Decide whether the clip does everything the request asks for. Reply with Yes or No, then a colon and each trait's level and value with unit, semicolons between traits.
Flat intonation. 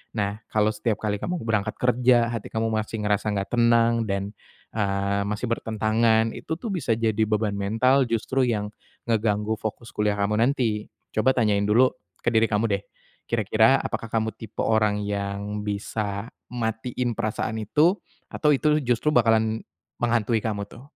Yes: narrow, 2.2 semitones